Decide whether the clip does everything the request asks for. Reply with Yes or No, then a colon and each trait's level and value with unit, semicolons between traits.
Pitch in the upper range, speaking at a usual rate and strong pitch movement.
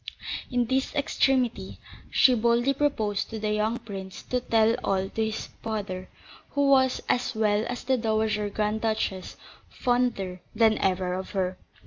No: high, 220 Hz; average, 150 wpm; average, 3.2 semitones